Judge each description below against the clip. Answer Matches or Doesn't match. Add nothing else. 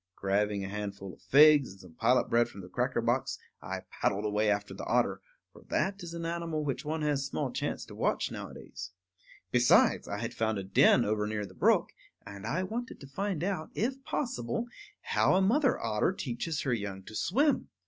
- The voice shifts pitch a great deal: Matches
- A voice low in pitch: Matches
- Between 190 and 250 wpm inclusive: Matches